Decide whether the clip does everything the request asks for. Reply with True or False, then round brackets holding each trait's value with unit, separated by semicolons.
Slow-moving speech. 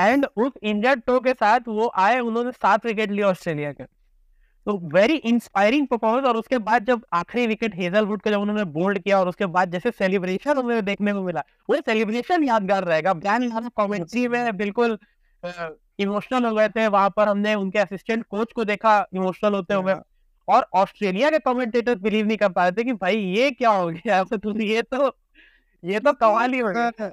False (120 wpm)